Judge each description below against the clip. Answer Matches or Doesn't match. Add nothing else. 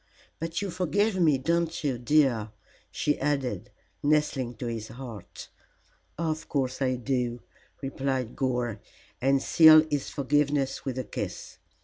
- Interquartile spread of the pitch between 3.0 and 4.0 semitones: Matches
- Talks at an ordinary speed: Doesn't match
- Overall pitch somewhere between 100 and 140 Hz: Matches